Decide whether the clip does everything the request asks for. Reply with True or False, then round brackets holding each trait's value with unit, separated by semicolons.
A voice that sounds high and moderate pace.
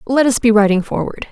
False (230 Hz; 230 wpm)